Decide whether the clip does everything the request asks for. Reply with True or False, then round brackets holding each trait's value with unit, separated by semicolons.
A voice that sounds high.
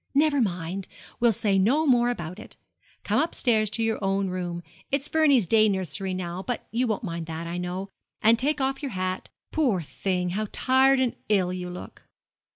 True (205 Hz)